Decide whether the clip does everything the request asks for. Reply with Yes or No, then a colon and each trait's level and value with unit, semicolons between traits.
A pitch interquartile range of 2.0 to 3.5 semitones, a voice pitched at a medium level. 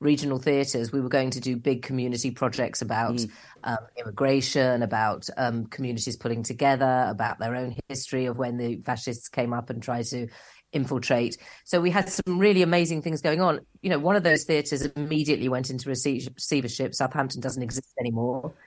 No: average, 2.7 semitones; low, 130 Hz